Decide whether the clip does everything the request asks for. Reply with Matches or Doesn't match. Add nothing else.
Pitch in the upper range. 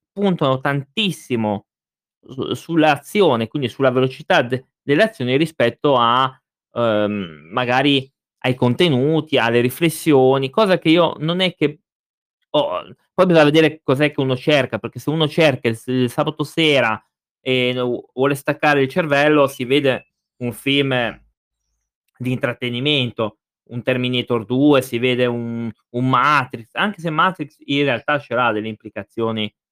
Doesn't match